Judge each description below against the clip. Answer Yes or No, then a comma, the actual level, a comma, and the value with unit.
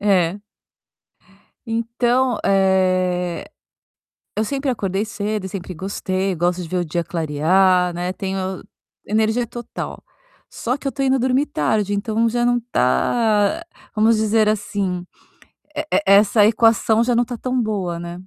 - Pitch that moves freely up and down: No, average, 4.1 semitones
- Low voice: No, high, 205 Hz